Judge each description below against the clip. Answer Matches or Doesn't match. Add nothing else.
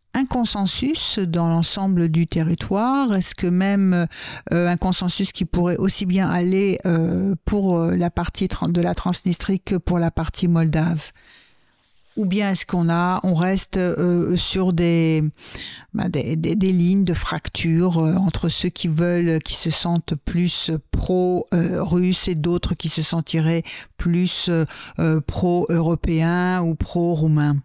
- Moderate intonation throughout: Doesn't match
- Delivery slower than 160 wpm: Matches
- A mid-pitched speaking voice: Matches